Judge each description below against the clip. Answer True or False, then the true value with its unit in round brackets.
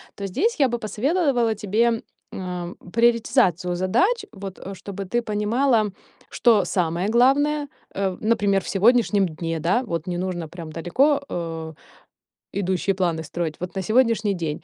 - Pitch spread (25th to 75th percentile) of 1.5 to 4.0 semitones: False (5.1 semitones)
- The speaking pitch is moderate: False (200 Hz)